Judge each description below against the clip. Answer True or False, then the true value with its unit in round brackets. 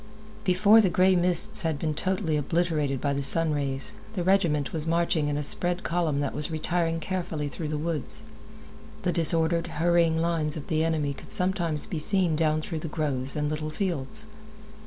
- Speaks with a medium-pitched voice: True (160 Hz)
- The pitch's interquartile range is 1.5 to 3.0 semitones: True (2.7 semitones)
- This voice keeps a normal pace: True (180 wpm)